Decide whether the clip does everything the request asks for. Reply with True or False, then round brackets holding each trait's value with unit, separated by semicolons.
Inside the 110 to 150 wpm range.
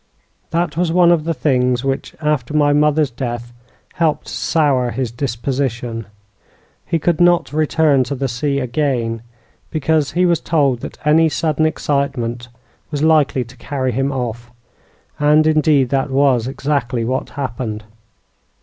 True (145 wpm)